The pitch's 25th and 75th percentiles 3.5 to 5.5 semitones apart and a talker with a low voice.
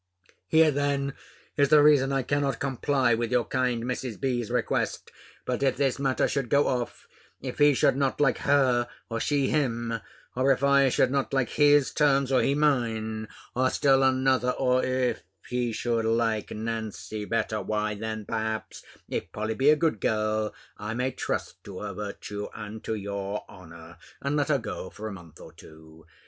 Yes: average, 3.9 semitones; low, 125 Hz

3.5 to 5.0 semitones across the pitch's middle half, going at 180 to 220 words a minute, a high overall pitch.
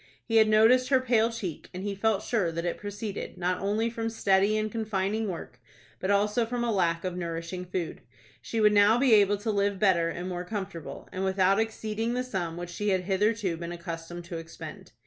Yes: average, 3.8 semitones; fast, 205 wpm; high, 200 Hz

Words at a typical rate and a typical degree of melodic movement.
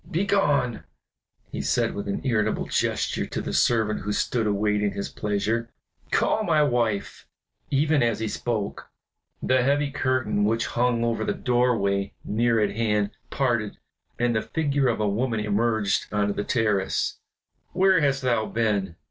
Yes: average, 150 wpm; average, 3.6 semitones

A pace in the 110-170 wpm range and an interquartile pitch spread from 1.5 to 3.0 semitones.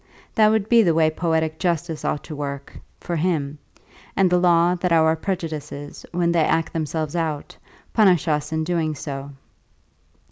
Yes: average, 165 wpm; narrow, 2.4 semitones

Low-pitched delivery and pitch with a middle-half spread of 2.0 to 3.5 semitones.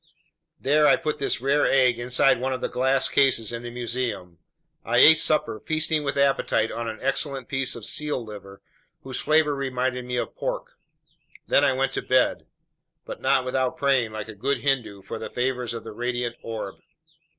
Yes: low, 125 Hz; average, 2.7 semitones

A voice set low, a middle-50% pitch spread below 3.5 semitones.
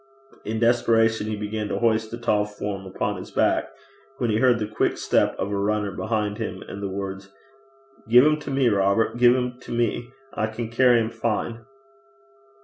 Yes: low, 110 Hz; narrow, 2.4 semitones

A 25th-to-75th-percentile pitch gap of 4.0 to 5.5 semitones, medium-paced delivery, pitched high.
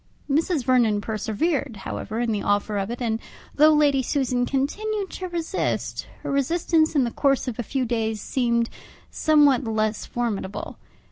Yes: average, 5.1 semitones; average, 155 wpm; very high, 250 Hz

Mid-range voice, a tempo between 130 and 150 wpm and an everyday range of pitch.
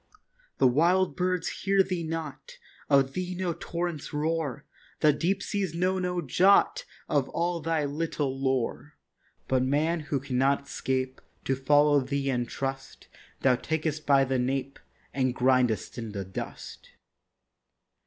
Yes: medium, 145 Hz; average, 140 wpm; average, 4.2 semitones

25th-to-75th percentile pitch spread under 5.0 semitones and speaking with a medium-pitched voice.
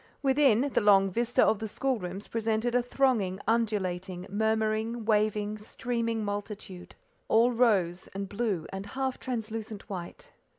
No: average, 2.9 semitones; high, 215 Hz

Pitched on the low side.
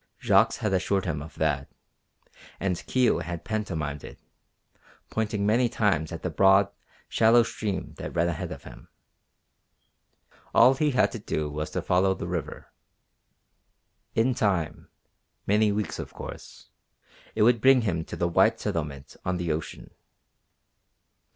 Yes: very low, 95 Hz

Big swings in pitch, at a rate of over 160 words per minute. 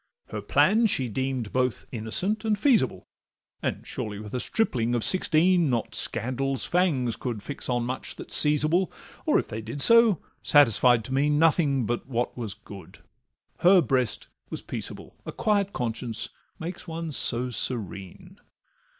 No: wide, 6.6 semitones; average, 155 wpm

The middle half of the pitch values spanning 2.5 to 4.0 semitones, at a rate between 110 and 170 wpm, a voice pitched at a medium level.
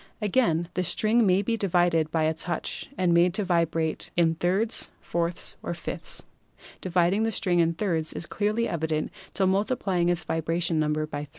No: average, 3.0 semitones; average, 180 wpm; medium, 175 Hz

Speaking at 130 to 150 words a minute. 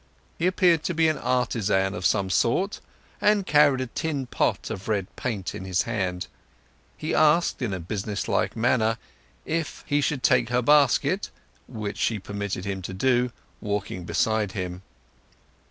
No: average, 160 wpm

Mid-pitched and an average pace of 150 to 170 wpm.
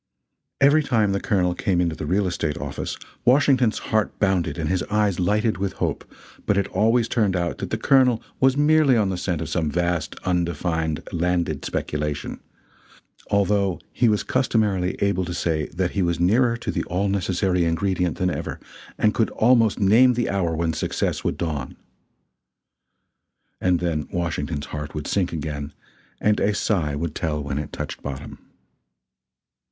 No: very low, 90 Hz; average, 165 wpm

